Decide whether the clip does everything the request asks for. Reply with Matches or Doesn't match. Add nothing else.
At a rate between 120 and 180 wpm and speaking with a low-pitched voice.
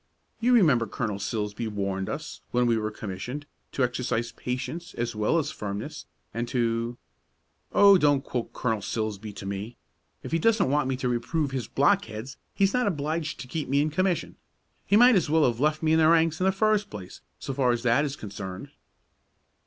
Doesn't match